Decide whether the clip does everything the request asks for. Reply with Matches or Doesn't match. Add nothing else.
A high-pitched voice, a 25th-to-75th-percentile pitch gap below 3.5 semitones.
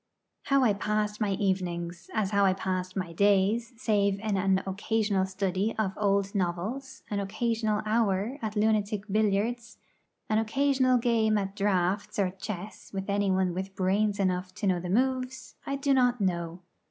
Matches